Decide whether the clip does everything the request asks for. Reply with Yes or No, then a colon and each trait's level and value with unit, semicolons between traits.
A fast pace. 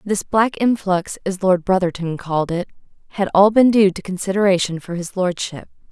No: average, 175 wpm